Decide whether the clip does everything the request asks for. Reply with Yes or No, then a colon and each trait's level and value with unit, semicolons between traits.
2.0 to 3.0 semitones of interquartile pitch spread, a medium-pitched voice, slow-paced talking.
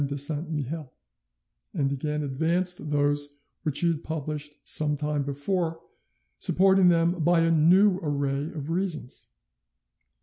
Yes: average, 2.7 semitones; medium, 155 Hz; slow, 130 wpm